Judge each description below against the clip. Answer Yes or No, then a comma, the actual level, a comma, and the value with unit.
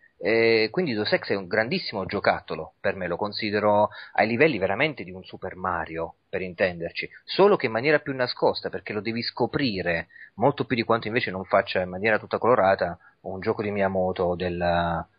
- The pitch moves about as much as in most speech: Yes, average, 4.1 semitones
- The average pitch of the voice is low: Yes, low, 105 Hz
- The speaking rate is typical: No, fast, 180 wpm